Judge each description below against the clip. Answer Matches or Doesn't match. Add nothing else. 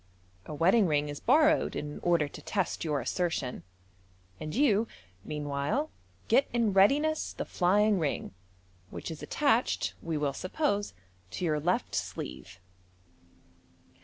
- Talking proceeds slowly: Matches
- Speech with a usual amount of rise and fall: Doesn't match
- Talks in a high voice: Doesn't match